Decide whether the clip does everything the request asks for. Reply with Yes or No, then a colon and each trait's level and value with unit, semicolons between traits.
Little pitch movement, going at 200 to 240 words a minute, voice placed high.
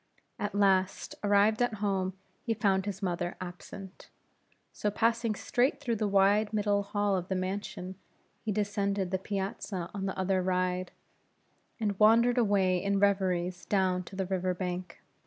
No: narrow, 1.9 semitones; average, 155 wpm; high, 195 Hz